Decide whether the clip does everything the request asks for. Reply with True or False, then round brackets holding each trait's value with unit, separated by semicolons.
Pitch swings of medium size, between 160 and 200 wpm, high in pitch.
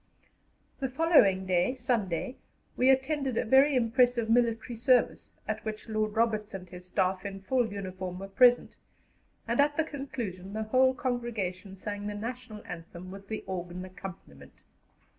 False (4.9 semitones; 150 wpm; 215 Hz)